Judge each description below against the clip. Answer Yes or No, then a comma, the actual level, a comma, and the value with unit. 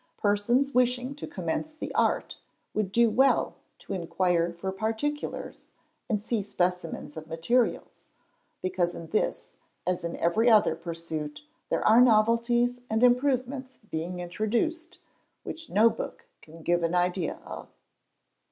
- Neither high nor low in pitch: No, high, 215 Hz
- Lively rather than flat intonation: Yes, wide, 6.0 semitones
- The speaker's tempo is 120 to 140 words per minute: Yes, slow, 135 wpm